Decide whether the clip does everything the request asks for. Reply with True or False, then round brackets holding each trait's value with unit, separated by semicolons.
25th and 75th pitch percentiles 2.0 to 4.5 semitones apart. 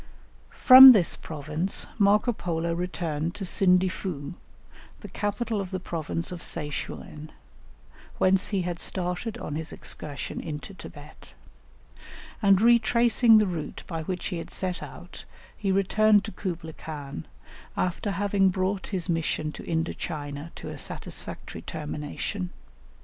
True (3.8 semitones)